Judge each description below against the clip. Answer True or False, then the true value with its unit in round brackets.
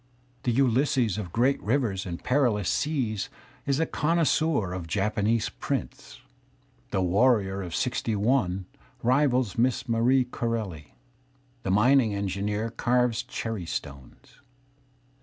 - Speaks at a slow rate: True (115 wpm)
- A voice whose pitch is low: True (115 Hz)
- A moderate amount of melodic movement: True (4.7 semitones)